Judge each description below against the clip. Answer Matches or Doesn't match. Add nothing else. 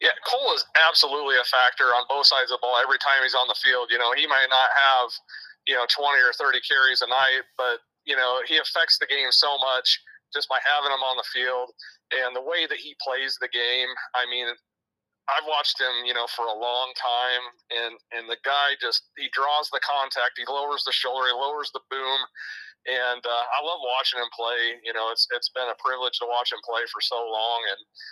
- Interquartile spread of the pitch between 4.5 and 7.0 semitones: Doesn't match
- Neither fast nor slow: Doesn't match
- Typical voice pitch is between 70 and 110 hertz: Doesn't match